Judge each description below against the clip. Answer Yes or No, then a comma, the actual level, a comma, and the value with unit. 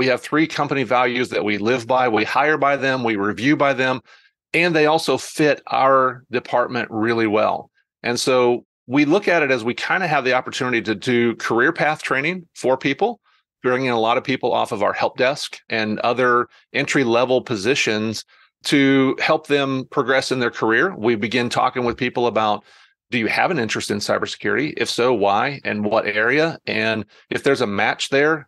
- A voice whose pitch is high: No, low, 125 Hz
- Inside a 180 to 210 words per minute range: Yes, average, 195 wpm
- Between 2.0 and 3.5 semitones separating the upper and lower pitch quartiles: Yes, average, 2.9 semitones